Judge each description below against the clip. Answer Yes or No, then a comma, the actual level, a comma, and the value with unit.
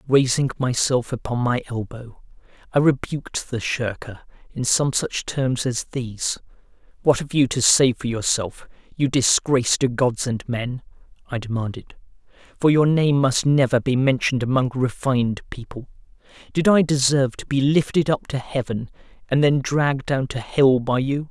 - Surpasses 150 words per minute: Yes, average, 160 wpm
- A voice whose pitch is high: No, low, 130 Hz